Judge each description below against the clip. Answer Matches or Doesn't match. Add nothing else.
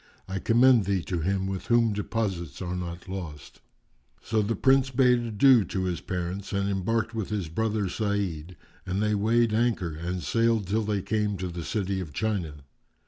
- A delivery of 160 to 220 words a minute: Matches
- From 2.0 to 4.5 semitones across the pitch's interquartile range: Matches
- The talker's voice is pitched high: Doesn't match